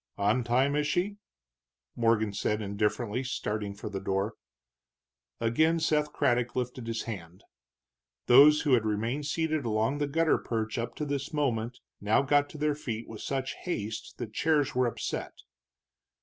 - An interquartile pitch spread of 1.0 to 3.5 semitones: No, average, 5.0 semitones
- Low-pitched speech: Yes, low, 120 Hz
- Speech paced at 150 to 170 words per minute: Yes, average, 155 wpm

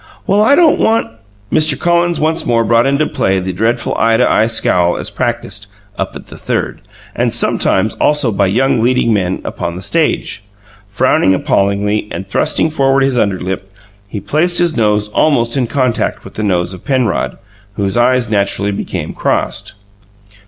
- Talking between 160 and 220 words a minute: Yes, average, 170 wpm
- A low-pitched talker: Yes, low, 115 Hz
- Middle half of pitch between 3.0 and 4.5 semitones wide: No, wide, 5.6 semitones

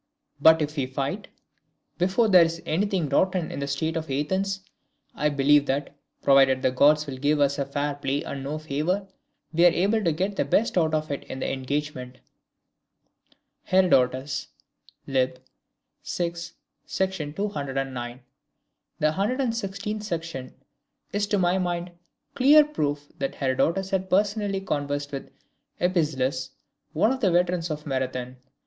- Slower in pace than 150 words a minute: Yes, average, 140 wpm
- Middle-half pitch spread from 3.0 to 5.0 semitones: No, wide, 5.4 semitones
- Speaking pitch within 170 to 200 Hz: No, medium, 155 Hz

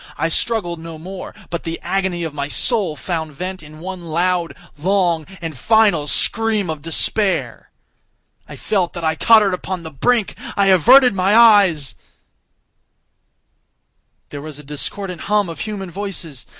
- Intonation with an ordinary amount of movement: Yes, average, 3.9 semitones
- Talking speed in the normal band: Yes, average, 145 wpm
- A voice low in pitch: No, medium, 180 Hz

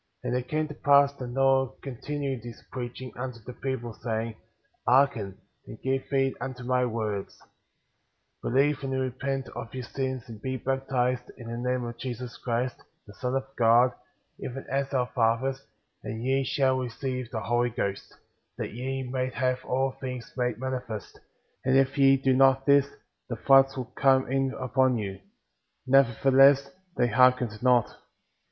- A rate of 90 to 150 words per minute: No, average, 165 wpm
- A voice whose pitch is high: No, low, 130 Hz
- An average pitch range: No, narrow, 1.9 semitones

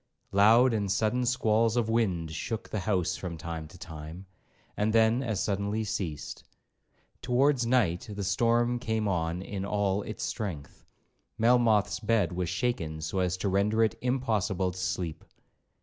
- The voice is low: Yes, low, 105 Hz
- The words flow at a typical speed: Yes, average, 150 wpm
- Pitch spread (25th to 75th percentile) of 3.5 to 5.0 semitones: Yes, average, 3.8 semitones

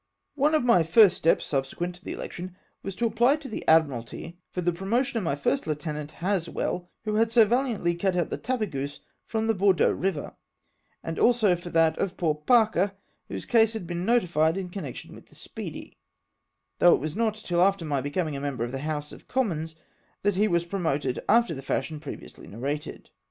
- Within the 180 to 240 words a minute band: Yes, average, 200 wpm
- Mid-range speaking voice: Yes, medium, 175 Hz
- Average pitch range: No, wide, 5.8 semitones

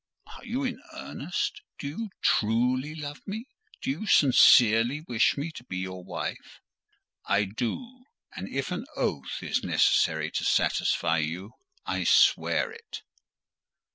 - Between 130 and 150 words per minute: Yes, average, 140 wpm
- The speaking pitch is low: Yes, low, 130 Hz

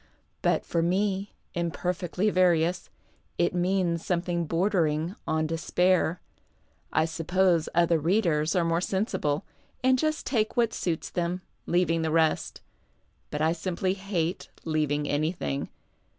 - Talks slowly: Yes, slow, 120 wpm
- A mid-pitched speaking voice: Yes, medium, 175 Hz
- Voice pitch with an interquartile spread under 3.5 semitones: Yes, narrow, 2.5 semitones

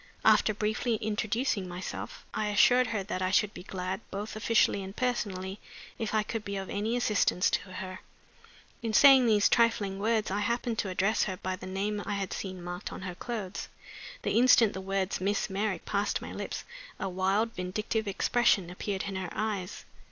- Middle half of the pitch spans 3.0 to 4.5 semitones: No, narrow, 2.5 semitones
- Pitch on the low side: No, high, 205 Hz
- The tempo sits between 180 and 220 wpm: Yes, average, 185 wpm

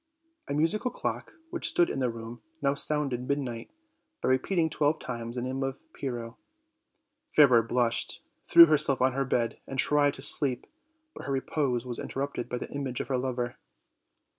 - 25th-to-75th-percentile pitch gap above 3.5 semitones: No, average, 2.8 semitones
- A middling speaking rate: Yes, average, 170 wpm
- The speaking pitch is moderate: No, low, 130 Hz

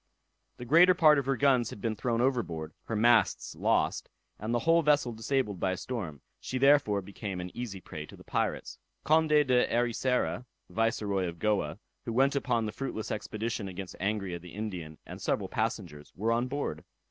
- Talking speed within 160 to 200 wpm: Yes, average, 180 wpm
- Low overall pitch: Yes, low, 115 Hz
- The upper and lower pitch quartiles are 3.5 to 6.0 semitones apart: Yes, average, 5.2 semitones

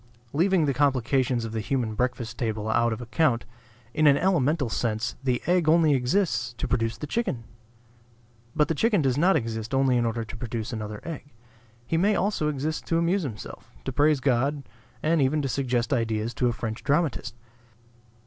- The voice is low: Yes, low, 130 Hz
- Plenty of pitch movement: No, average, 4.9 semitones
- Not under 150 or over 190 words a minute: Yes, average, 180 wpm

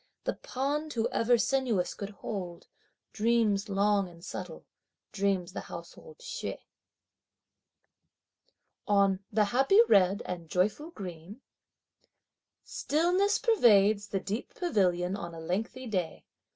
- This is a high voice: Yes, high, 205 Hz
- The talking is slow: Yes, slow, 110 wpm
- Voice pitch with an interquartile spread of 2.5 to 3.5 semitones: No, wide, 5.4 semitones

